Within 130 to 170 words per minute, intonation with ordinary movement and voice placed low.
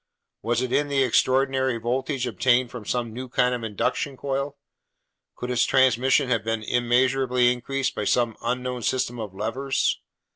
No: average, 155 wpm; narrow, 1.9 semitones; low, 125 Hz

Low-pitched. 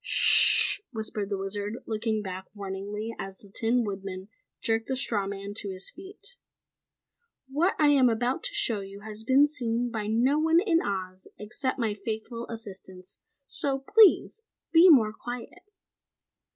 No: high, 225 Hz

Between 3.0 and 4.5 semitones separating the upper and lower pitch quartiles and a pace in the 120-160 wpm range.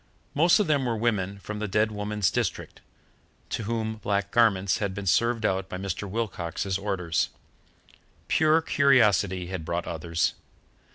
Yes: average, 3.4 semitones; average, 150 wpm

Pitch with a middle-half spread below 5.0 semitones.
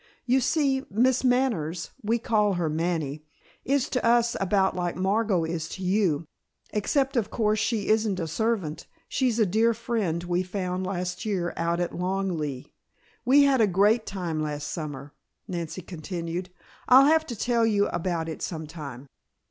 No: average, 5.3 semitones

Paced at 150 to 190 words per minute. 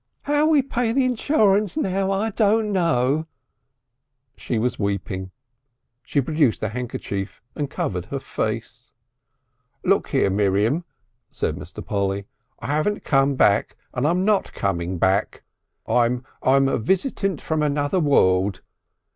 No: slow, 135 wpm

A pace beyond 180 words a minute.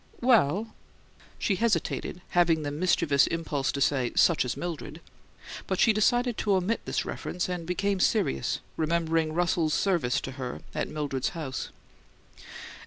No: average, 145 wpm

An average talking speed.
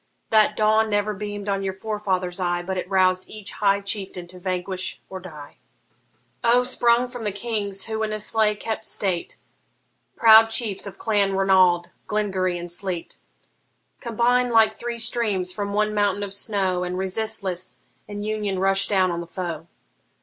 Yes: average, 160 wpm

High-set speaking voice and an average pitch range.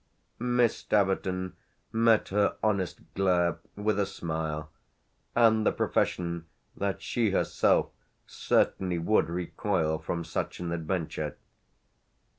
No: very low, 95 Hz; average, 3.8 semitones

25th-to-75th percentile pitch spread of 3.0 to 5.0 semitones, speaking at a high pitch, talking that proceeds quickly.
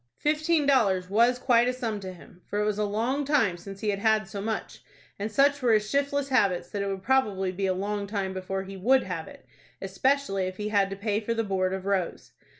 Yes: average, 4.4 semitones; high, 205 Hz; fast, 240 wpm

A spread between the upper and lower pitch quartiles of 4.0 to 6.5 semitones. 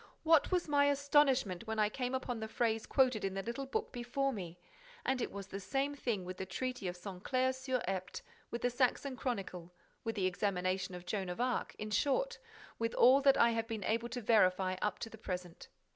Yes: average, 5.2 semitones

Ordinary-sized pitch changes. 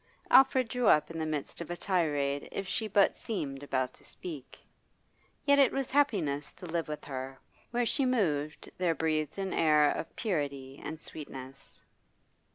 No: wide, 6.0 semitones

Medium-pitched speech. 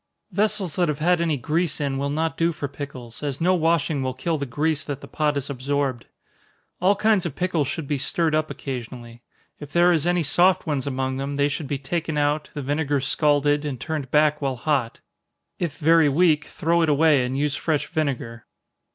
Yes: medium, 150 Hz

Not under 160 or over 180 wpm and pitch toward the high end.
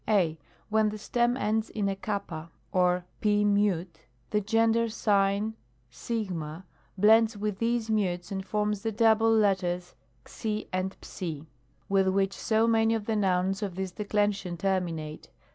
No: average, 145 wpm; high, 205 Hz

